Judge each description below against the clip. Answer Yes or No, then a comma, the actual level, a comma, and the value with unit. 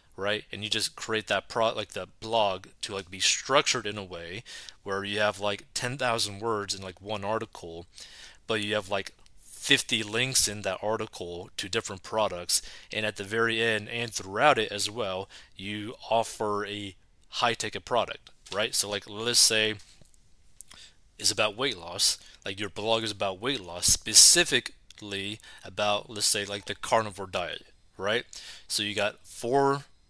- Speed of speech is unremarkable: Yes, average, 170 wpm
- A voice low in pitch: Yes, low, 105 Hz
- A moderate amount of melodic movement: No, narrow, 2.2 semitones